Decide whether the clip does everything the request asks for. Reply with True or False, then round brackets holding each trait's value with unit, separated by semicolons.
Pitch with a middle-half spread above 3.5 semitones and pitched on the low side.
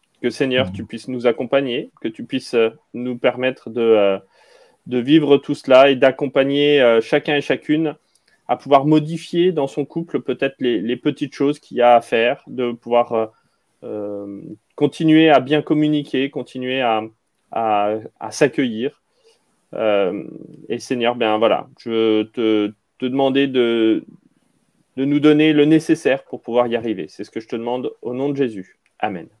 True (3.9 semitones; 130 Hz)